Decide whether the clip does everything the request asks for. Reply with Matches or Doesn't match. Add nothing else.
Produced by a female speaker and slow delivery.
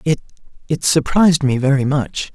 Doesn't match